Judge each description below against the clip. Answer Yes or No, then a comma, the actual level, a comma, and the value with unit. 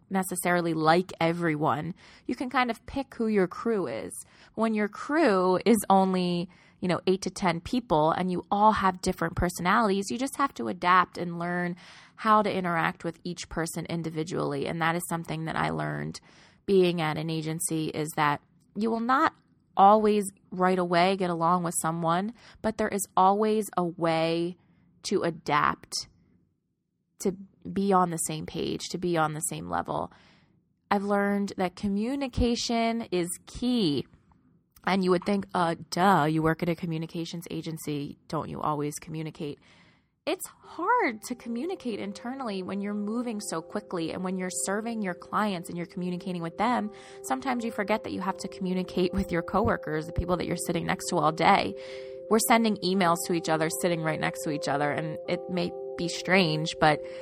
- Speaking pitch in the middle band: Yes, medium, 180 Hz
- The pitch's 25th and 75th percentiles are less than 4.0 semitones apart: Yes, average, 3.5 semitones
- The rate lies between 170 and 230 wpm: Yes, average, 175 wpm